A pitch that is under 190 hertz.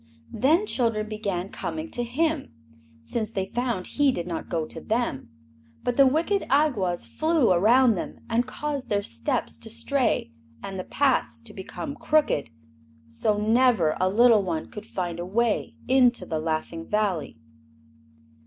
No: high, 225 Hz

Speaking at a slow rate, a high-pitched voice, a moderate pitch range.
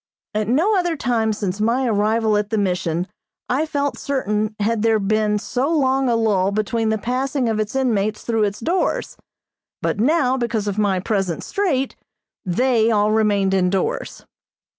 No: average, 160 wpm; high, 220 Hz; average, 3.8 semitones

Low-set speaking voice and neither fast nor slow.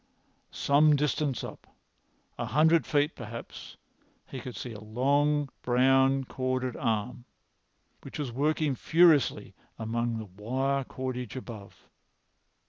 No: low, 130 Hz; slow, 105 wpm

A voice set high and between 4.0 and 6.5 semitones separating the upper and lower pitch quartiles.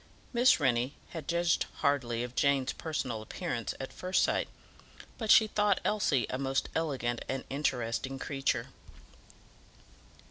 No: low, 135 Hz; average, 5.2 semitones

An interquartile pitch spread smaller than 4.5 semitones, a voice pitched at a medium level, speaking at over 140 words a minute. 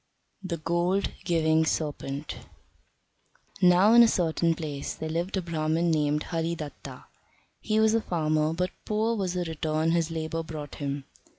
Yes: narrow, 2.5 semitones; medium, 165 Hz; average, 150 wpm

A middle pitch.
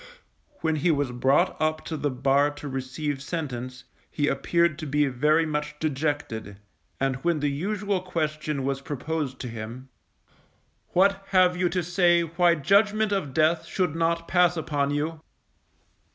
Yes: medium, 155 Hz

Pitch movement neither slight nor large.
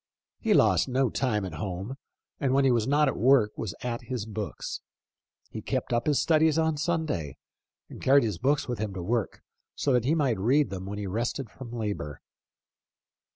Yes: average, 5.0 semitones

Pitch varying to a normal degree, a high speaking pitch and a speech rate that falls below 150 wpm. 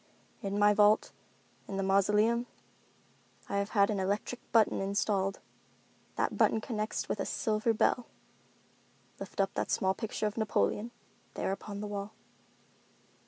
No: narrow, 1.5 semitones; high, 205 Hz; slow, 135 wpm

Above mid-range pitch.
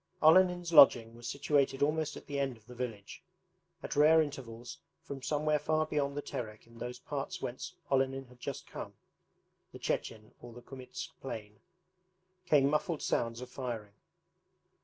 No: low, 135 Hz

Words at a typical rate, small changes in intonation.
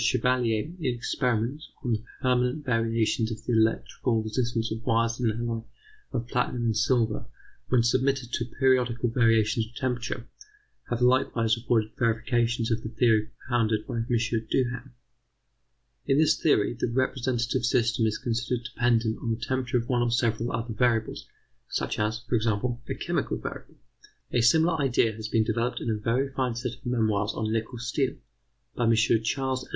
Yes: average, 165 wpm; narrow, 1.8 semitones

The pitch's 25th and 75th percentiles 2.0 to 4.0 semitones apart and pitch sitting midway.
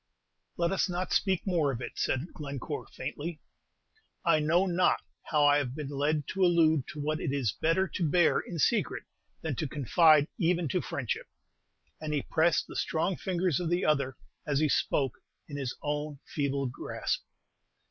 Yes: average, 3.3 semitones; medium, 155 Hz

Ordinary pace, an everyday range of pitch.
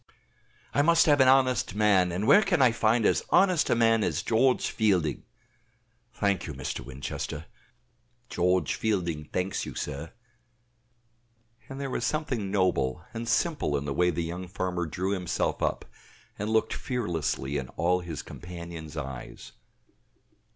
No: average, 150 wpm; wide, 5.9 semitones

